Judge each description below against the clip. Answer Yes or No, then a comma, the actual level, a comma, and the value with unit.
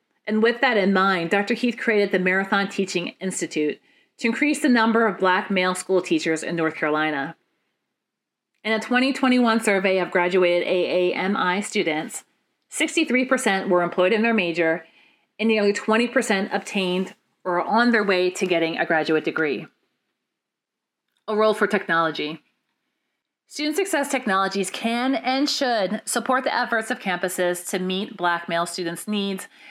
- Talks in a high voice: Yes, high, 200 Hz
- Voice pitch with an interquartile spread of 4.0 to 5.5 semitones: Yes, average, 4.6 semitones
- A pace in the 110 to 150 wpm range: Yes, average, 145 wpm